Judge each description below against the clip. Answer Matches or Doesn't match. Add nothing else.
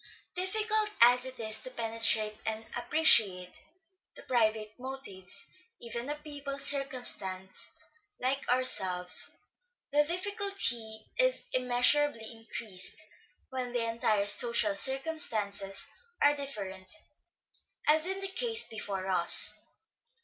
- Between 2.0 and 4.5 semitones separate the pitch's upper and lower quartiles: Doesn't match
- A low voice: Doesn't match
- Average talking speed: Doesn't match